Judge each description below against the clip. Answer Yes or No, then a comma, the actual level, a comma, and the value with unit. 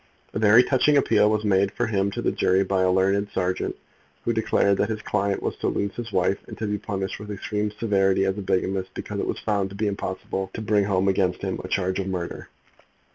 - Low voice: Yes, low, 100 Hz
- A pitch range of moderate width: No, narrow, 1.6 semitones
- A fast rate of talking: Yes, fast, 235 wpm